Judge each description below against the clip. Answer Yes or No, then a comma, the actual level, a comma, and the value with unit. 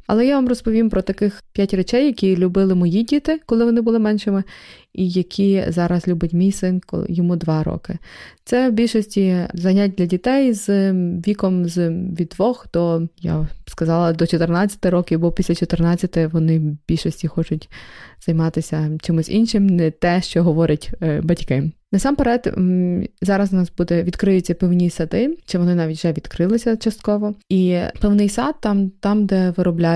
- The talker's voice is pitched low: No, medium, 185 Hz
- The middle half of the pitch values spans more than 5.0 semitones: No, average, 3.3 semitones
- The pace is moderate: No, fast, 160 wpm